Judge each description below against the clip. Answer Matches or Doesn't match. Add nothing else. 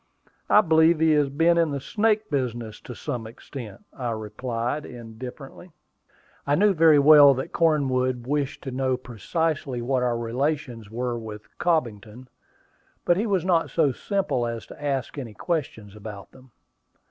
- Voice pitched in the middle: Doesn't match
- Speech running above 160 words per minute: Doesn't match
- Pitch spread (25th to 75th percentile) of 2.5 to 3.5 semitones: Doesn't match